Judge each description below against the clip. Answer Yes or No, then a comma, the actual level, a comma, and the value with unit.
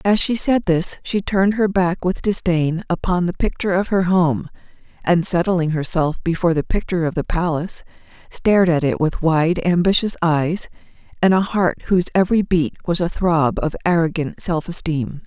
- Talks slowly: No, average, 175 wpm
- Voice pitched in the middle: Yes, medium, 175 Hz